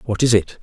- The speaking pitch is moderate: No, low, 110 Hz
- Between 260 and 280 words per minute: No, fast, 290 wpm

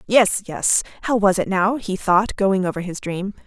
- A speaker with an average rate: No, fast, 210 wpm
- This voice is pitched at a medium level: No, high, 195 Hz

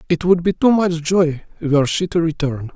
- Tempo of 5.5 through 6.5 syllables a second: No, 5.1 syllables/s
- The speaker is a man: Yes, male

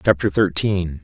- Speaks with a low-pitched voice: Yes, very low, 90 Hz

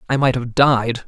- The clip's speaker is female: No, male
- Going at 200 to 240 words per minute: Yes, fast, 225 wpm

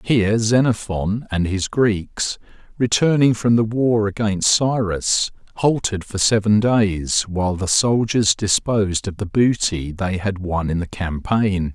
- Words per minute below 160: Yes, average, 145 wpm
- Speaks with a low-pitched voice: Yes, low, 105 Hz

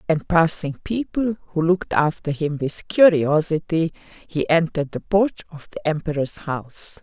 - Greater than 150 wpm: No, average, 145 wpm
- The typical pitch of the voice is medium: Yes, medium, 165 Hz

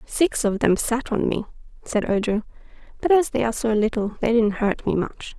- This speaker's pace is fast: Yes, fast, 210 wpm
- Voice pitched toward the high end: Yes, high, 225 Hz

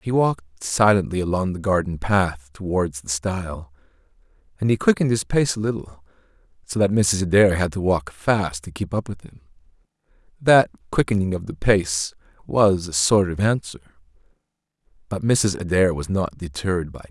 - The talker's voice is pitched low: Yes, very low, 95 Hz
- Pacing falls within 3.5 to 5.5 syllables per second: Yes, 5.0 syllables/s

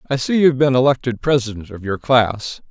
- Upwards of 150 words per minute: Yes, average, 200 wpm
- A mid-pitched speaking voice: No, low, 125 Hz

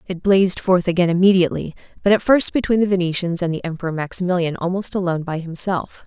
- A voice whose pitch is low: No, medium, 180 Hz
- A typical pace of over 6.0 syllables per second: Yes, 6.6 syllables/s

